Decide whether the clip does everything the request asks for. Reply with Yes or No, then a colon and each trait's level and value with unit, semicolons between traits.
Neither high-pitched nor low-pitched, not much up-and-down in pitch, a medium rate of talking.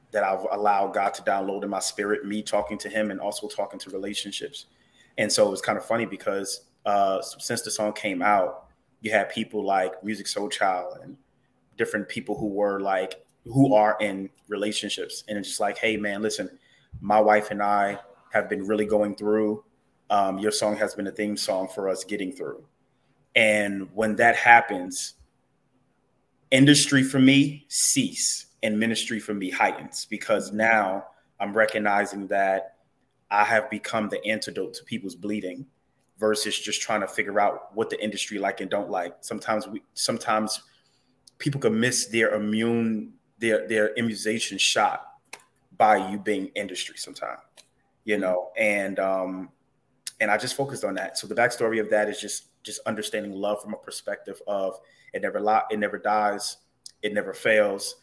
No: low, 105 Hz; narrow, 1.8 semitones; average, 170 wpm